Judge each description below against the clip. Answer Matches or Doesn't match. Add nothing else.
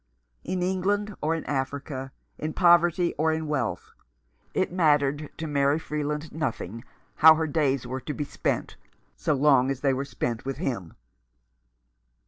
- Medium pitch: Matches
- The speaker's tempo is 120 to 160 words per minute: Matches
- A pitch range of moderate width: Matches